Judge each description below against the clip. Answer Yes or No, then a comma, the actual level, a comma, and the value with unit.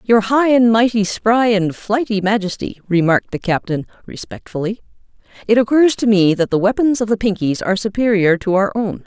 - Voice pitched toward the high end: Yes, high, 210 Hz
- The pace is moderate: Yes, average, 180 wpm